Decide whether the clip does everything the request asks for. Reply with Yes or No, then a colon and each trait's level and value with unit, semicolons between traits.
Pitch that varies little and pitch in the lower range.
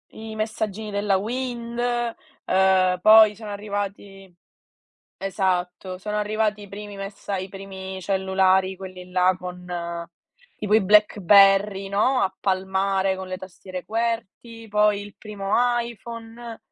No: narrow, 2.1 semitones; high, 200 Hz